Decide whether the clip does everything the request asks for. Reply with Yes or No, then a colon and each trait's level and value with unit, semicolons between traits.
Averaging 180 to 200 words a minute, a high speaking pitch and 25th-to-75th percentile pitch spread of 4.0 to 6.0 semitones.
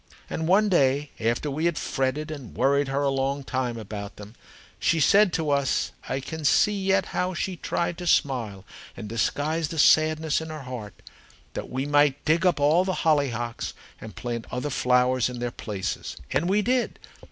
No: average, 185 wpm; medium, 145 Hz; average, 4.3 semitones